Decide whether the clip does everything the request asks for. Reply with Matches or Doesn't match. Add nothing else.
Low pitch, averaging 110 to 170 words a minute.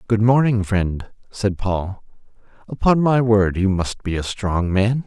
Matches